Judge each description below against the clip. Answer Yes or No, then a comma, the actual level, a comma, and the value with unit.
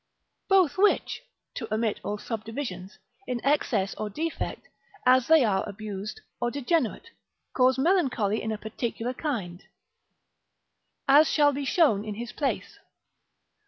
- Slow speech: Yes, slow, 125 wpm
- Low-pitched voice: No, high, 240 Hz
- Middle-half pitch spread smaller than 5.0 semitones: No, average, 5.3 semitones